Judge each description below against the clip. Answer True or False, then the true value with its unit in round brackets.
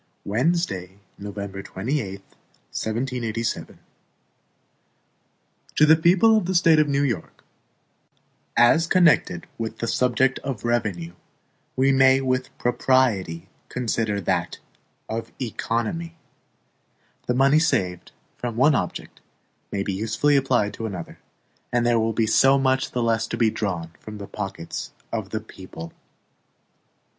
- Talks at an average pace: False (130 wpm)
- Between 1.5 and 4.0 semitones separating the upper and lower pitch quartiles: False (4.6 semitones)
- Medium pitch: False (120 Hz)